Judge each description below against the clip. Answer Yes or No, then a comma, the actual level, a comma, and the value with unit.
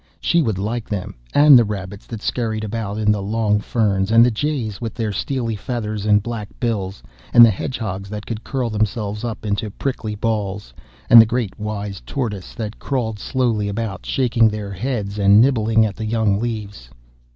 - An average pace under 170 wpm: No, average, 185 wpm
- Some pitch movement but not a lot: No, narrow, 2.3 semitones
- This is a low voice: Yes, low, 110 Hz